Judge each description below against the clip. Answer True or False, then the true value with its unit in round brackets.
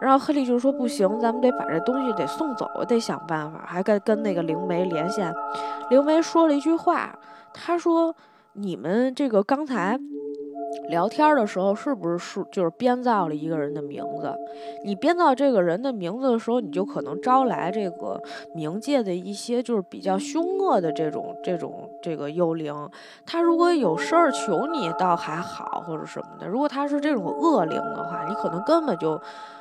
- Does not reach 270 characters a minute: False (280 characters per minute)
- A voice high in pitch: True (230 Hz)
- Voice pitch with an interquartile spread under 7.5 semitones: False (8.0 semitones)